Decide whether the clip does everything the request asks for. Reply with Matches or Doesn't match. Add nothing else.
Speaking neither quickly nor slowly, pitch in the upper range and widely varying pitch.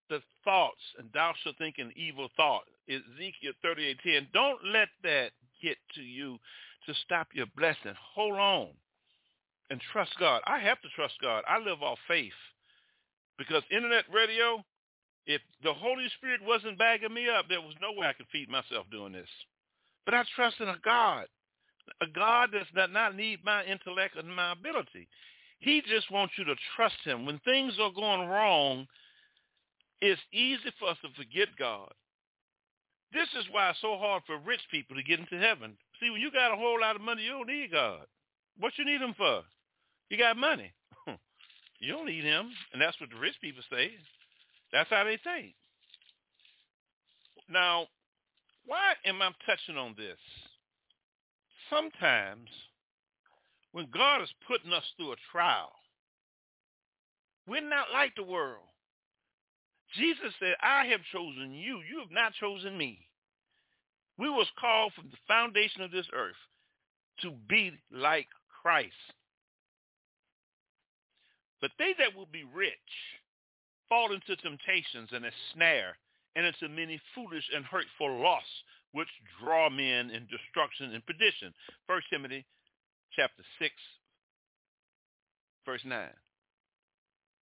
Matches